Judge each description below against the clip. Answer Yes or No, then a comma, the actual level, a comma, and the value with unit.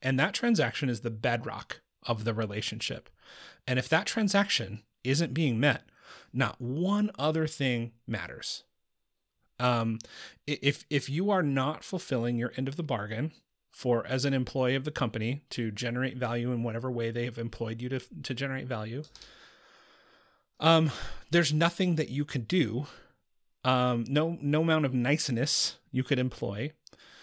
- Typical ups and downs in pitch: Yes, average, 4.2 semitones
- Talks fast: No, average, 155 wpm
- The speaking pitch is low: Yes, low, 130 Hz